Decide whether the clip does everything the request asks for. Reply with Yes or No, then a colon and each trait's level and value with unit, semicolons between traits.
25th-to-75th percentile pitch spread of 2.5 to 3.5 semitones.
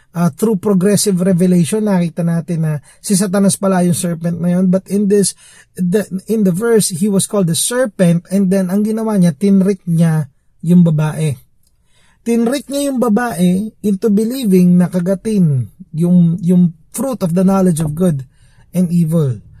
Yes: average, 3.2 semitones